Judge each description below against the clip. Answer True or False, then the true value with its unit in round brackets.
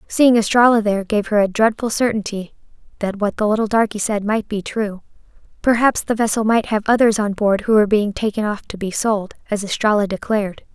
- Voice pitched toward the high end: True (210 Hz)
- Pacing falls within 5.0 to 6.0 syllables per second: True (5.7 syllables/s)